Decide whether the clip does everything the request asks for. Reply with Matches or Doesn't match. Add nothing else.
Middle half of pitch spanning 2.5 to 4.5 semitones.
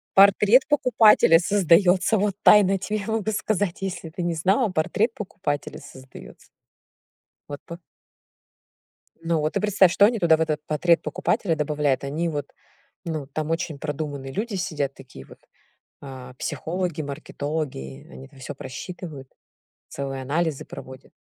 Doesn't match